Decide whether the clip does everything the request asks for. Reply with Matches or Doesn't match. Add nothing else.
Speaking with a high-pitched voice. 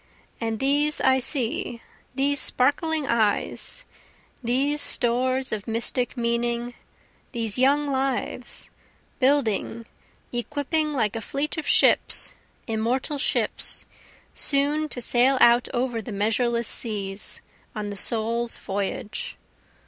Matches